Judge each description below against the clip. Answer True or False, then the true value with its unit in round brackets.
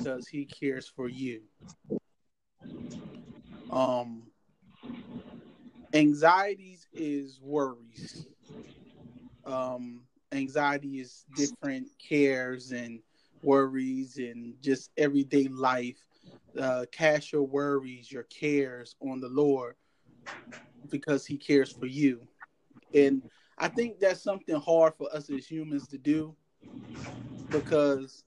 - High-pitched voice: False (140 Hz)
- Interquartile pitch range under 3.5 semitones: True (3.1 semitones)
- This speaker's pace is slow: True (100 wpm)